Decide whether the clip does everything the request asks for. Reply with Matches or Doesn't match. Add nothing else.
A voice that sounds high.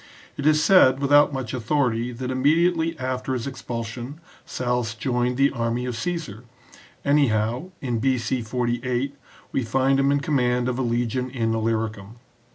Doesn't match